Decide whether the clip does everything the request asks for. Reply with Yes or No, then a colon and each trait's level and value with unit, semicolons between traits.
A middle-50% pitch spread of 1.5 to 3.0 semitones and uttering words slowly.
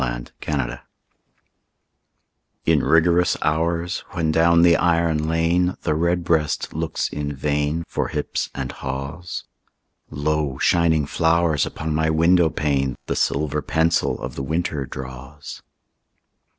Yes: narrow, 2.6 semitones; slow, 115 wpm